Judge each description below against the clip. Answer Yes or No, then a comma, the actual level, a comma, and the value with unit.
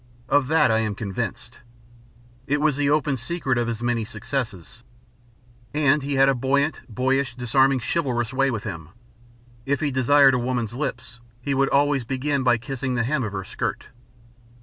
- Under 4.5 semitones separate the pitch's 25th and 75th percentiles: Yes, average, 3.0 semitones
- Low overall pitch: Yes, low, 130 Hz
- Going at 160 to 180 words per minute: Yes, average, 170 wpm